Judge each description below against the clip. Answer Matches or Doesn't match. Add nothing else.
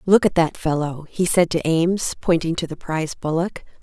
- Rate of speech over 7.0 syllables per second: Doesn't match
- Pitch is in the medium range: Matches